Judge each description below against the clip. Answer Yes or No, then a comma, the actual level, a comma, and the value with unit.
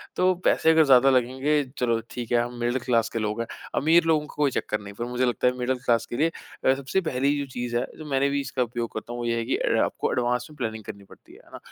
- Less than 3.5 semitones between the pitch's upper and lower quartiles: Yes, average, 2.8 semitones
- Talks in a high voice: No, low, 125 Hz